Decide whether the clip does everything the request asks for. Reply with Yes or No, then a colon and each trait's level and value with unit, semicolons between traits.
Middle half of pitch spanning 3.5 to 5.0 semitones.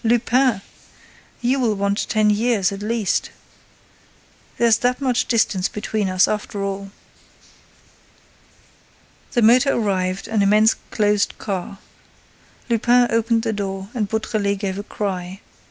No: average, 2.8 semitones